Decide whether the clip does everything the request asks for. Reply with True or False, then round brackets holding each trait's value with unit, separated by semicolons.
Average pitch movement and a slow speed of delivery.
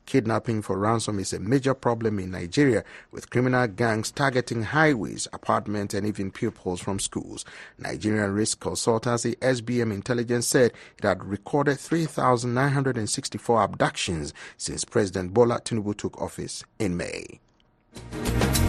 True (3.5 semitones; 125 wpm)